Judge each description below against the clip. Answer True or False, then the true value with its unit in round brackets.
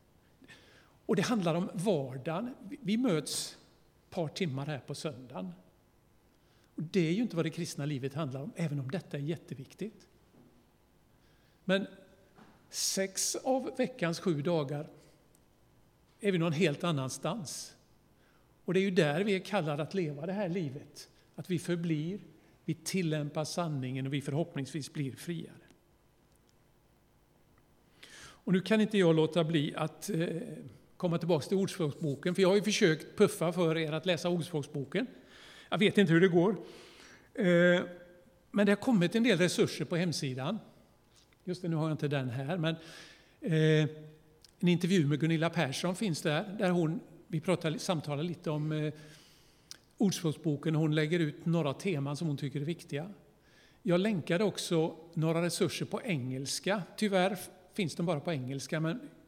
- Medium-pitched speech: True (165 Hz)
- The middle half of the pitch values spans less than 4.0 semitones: True (3.6 semitones)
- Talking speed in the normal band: True (150 wpm)